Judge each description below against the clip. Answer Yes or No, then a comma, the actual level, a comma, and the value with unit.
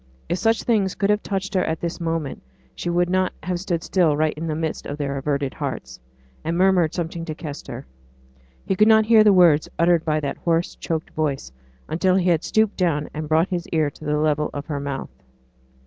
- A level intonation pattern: No, average, 3.4 semitones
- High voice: No, medium, 165 Hz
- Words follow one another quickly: Yes, fast, 210 wpm